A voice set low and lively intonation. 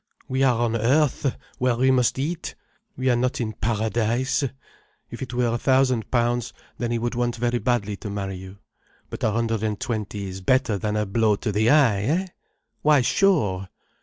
No: low, 120 Hz; average, 3.3 semitones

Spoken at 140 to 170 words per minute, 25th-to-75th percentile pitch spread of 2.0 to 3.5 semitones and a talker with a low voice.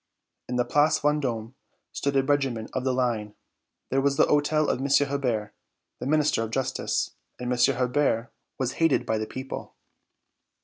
Yes: average, 165 wpm; average, 2.9 semitones; low, 130 Hz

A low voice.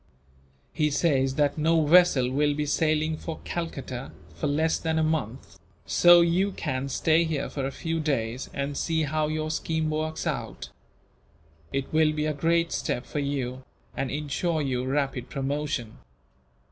No: medium, 150 Hz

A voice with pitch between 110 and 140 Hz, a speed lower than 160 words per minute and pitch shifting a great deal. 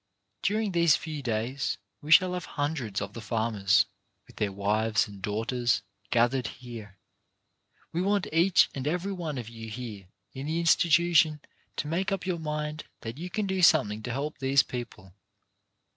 No: low, 135 Hz; average, 165 wpm; wide, 6.9 semitones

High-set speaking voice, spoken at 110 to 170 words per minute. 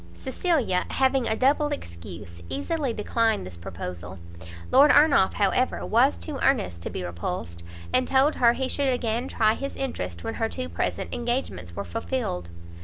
Yes: high, 230 Hz; average, 160 wpm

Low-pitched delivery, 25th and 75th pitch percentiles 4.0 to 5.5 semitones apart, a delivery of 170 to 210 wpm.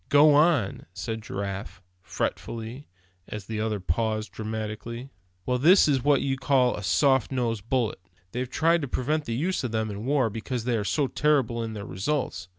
Yes: low, 120 Hz; average, 4.3 semitones; average, 180 wpm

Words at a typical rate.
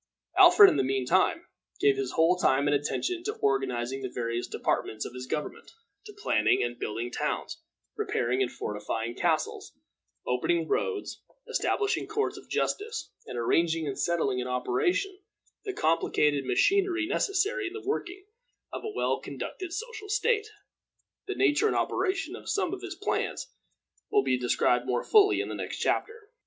Yes: average, 160 wpm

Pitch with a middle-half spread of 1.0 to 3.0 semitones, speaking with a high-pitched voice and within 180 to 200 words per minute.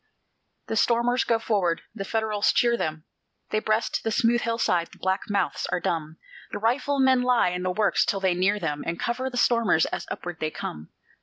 No: average, 5.0 semitones; high, 210 Hz; average, 190 wpm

